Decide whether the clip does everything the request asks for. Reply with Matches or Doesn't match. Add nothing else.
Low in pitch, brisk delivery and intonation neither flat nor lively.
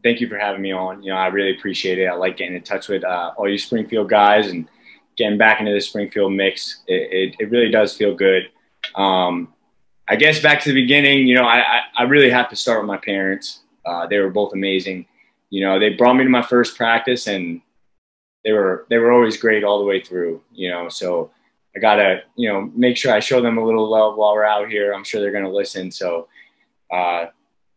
Matches